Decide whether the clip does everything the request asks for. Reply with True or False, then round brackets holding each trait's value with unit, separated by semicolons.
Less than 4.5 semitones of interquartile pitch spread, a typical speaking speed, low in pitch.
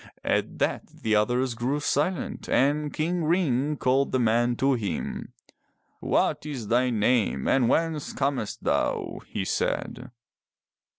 False (3.7 semitones; 130 wpm; 130 Hz)